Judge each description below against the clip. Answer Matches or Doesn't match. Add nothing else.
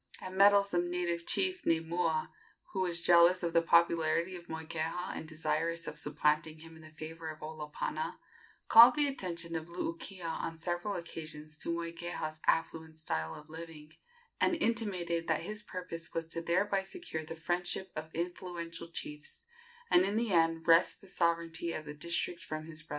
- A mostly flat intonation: Matches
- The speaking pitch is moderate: Matches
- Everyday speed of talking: Matches